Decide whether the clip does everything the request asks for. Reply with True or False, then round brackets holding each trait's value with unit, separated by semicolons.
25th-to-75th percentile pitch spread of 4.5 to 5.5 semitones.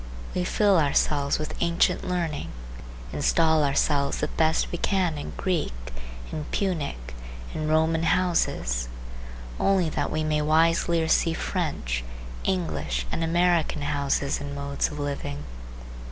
False (3.1 semitones)